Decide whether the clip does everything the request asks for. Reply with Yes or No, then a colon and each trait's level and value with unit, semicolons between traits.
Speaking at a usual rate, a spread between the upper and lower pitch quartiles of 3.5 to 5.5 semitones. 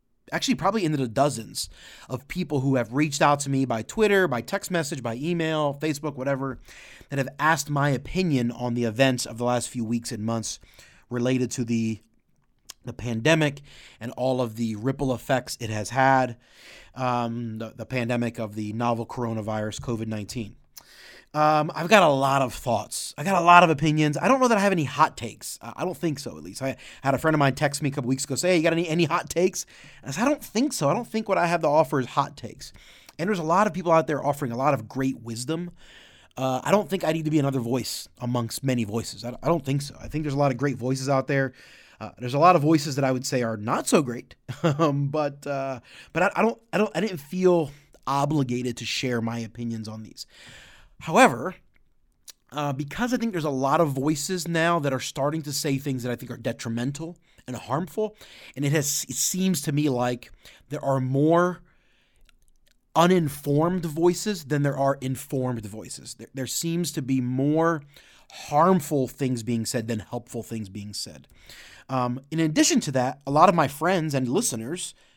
No: fast, 215 wpm; average, 4.8 semitones